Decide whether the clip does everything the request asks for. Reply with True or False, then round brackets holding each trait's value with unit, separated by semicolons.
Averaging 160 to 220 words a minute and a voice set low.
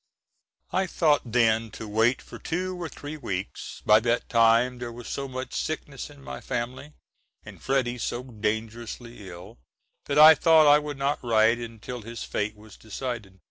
True (170 wpm; 120 Hz)